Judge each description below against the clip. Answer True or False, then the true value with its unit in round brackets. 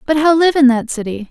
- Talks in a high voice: True (270 Hz)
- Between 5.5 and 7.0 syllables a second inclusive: True (6.0 syllables/s)